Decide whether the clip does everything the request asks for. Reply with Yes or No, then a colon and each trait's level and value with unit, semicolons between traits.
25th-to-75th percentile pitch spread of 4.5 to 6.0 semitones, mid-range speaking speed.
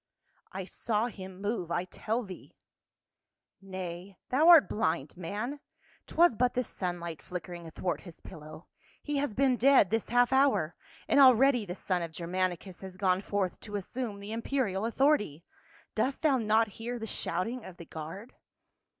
Yes: wide, 5.5 semitones; average, 165 wpm